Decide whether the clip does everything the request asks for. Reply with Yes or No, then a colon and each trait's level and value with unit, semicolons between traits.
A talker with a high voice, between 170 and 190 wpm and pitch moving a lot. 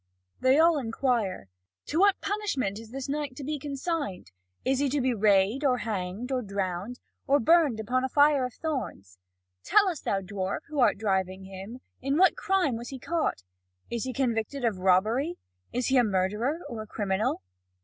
Yes: very high, 250 Hz; average, 180 wpm; wide, 6.1 semitones